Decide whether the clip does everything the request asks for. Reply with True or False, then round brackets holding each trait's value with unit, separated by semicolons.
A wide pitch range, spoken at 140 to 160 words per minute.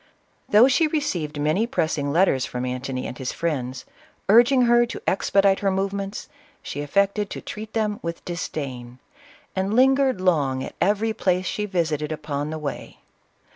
True (6.3 semitones; 155 wpm)